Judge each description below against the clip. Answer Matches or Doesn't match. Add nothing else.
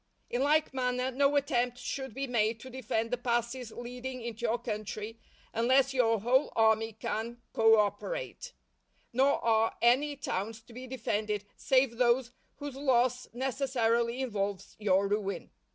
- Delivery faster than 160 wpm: Doesn't match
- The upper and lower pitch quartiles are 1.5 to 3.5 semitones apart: Matches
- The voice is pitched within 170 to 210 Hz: Doesn't match